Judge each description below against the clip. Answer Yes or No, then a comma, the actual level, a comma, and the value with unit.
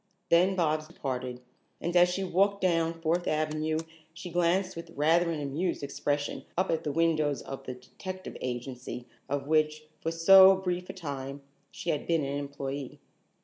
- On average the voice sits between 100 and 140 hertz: No, medium, 160 Hz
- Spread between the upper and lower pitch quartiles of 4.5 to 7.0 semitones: No, average, 3.7 semitones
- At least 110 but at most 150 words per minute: No, average, 165 wpm